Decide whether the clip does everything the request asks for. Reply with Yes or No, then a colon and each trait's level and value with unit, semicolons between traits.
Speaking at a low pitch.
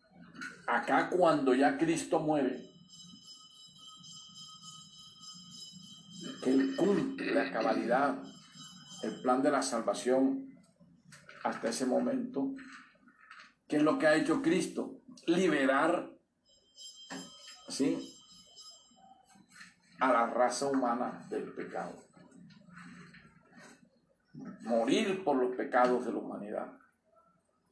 No: medium, 180 Hz